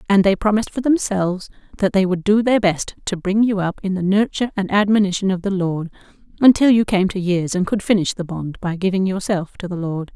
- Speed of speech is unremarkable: No, fast, 230 wpm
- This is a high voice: Yes, high, 195 Hz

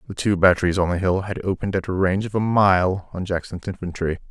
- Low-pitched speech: Yes, very low, 95 Hz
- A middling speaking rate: No, fast, 235 wpm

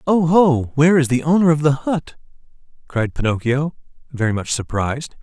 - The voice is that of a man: Yes, male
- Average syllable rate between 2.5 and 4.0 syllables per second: No, 5.3 syllables/s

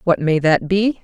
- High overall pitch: No, medium, 175 Hz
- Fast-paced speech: Yes, fast, 235 wpm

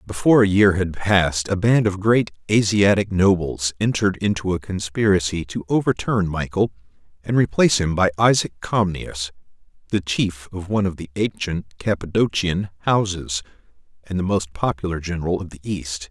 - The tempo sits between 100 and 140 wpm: No, average, 155 wpm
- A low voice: Yes, very low, 95 Hz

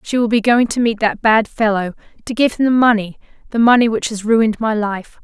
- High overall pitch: Yes, high, 225 Hz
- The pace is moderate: No, fast, 230 wpm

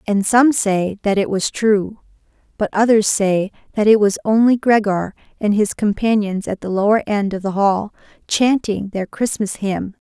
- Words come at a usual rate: Yes, average, 175 wpm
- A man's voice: No, female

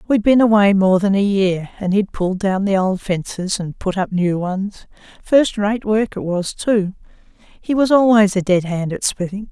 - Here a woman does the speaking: Yes, female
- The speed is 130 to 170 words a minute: No, average, 200 wpm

